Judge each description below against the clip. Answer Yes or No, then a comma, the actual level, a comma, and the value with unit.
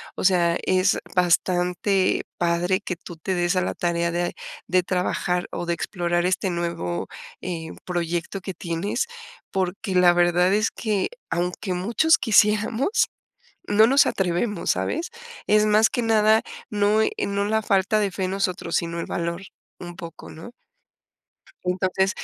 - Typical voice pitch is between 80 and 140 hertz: No, medium, 185 Hz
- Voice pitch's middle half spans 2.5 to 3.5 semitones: Yes, average, 2.9 semitones